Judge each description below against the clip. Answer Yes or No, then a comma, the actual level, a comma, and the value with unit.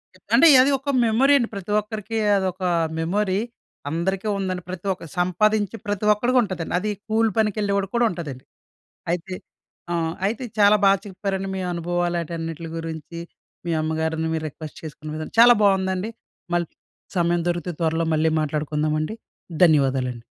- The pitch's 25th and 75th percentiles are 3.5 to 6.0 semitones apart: Yes, average, 4.2 semitones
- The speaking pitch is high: No, medium, 180 Hz